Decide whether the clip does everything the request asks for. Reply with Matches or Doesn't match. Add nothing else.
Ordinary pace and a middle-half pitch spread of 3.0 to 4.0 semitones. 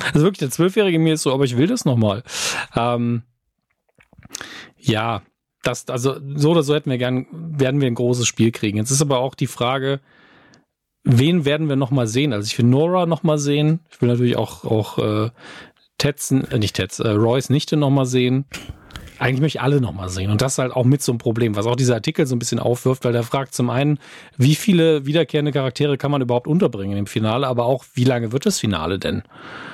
Doesn't match